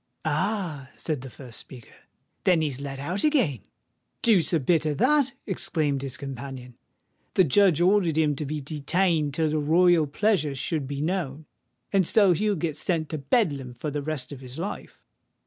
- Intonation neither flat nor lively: Yes, average, 4.6 semitones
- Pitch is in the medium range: Yes, medium, 155 Hz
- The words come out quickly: No, average, 175 wpm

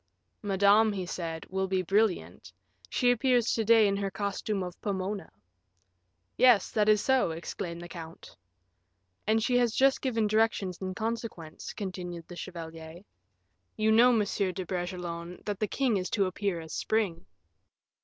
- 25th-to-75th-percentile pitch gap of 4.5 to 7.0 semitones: No, average, 3.7 semitones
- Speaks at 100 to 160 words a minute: Yes, average, 155 wpm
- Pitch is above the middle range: Yes, high, 195 Hz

